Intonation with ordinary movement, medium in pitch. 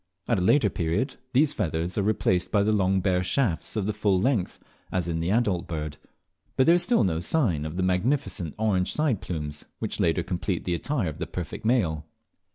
No: average, 4.6 semitones; very low, 95 Hz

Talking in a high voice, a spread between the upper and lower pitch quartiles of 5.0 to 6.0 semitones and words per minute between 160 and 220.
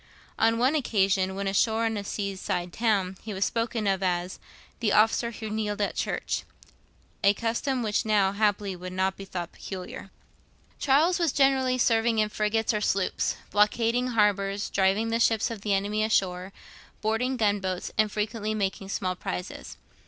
No: high, 210 Hz; average, 2.7 semitones; average, 165 wpm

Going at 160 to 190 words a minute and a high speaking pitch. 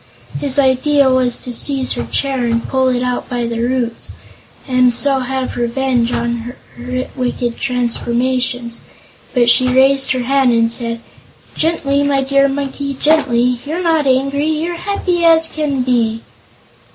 No: average, 150 wpm; very high, 260 Hz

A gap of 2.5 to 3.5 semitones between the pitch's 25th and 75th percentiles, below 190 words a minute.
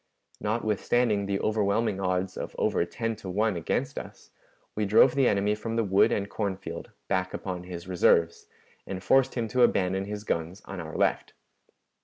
Yes: average, 2.9 semitones; average, 175 wpm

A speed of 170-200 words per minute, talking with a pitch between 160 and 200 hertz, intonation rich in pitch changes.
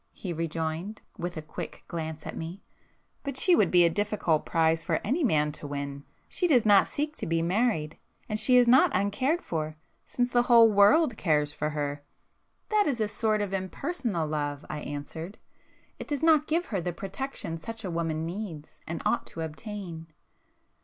Yes: average, 175 wpm; medium, 185 Hz; wide, 6.8 semitones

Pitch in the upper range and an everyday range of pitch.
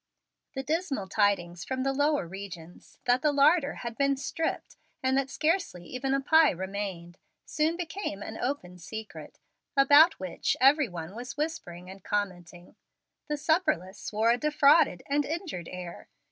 No: very high, 255 Hz; wide, 7.9 semitones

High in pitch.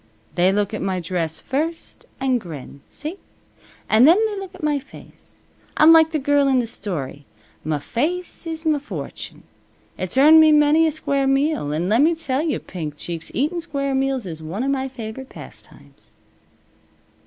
Yes: very high, 270 Hz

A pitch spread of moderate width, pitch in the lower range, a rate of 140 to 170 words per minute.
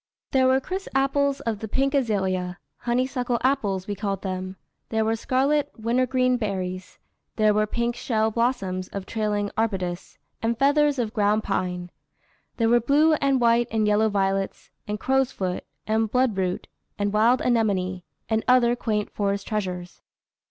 No: average, 4.3 semitones; high, 220 Hz; average, 150 wpm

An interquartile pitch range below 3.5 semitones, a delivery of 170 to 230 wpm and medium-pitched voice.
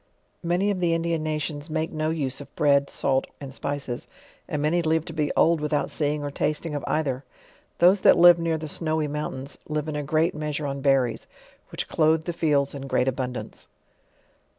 Yes: narrow, 2.4 semitones; average, 190 wpm; medium, 150 Hz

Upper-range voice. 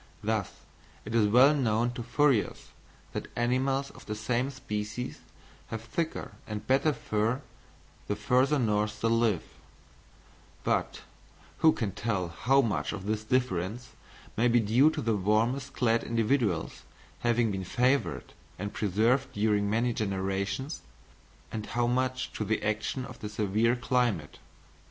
No: low, 115 Hz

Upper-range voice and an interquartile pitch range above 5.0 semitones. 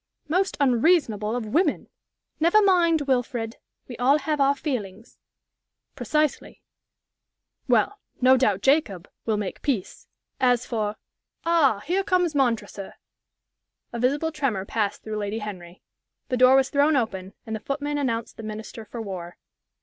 Yes: very high, 250 Hz; wide, 5.5 semitones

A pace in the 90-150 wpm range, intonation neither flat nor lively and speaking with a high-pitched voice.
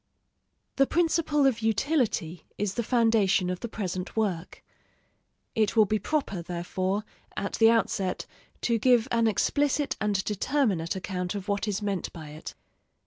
Yes: average, 145 wpm; average, 4.1 semitones; high, 210 Hz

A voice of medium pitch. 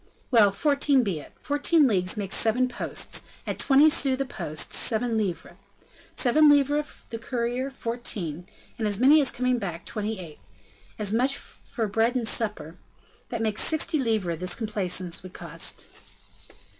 No: high, 230 Hz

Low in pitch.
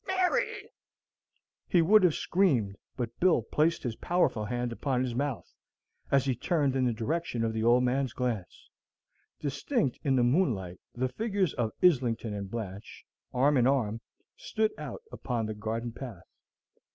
Yes: low, 125 Hz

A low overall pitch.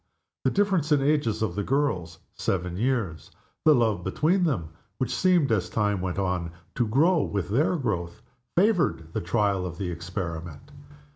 Yes: low, 105 Hz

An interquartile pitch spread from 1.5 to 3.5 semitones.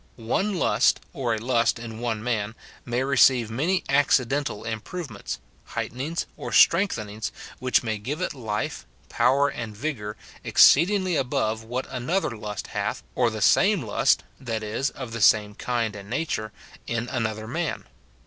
No: average, 4.1 semitones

